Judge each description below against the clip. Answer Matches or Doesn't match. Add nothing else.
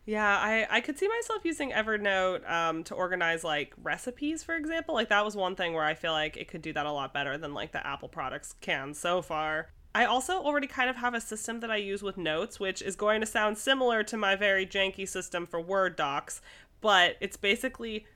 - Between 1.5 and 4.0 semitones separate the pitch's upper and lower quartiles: Doesn't match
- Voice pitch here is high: Matches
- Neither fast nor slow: Doesn't match